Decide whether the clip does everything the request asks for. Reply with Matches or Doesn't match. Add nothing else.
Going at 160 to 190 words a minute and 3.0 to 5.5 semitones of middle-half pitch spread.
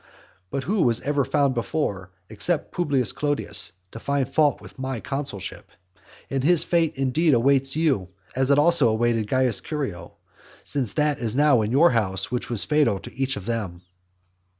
Matches